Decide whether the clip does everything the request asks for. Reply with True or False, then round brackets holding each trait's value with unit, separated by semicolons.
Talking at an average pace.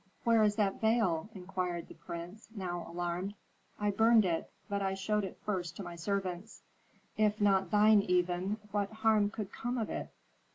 True (170 wpm)